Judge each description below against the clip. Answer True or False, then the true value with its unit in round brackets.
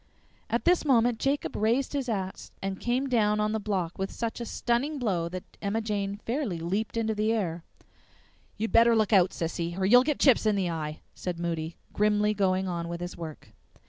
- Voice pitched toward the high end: True (210 Hz)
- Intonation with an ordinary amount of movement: True (4.5 semitones)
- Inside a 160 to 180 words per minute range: False (200 wpm)